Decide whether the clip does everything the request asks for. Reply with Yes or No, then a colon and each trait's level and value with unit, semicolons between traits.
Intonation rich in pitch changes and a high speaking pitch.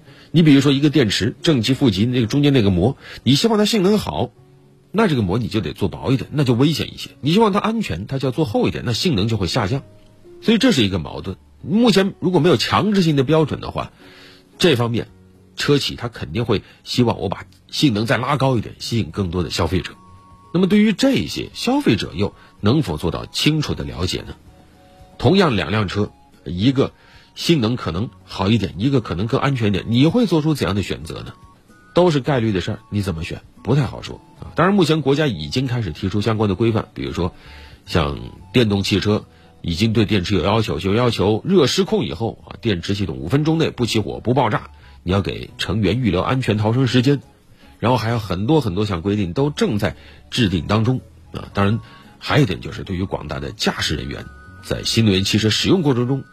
No: wide, 6.4 semitones; low, 115 Hz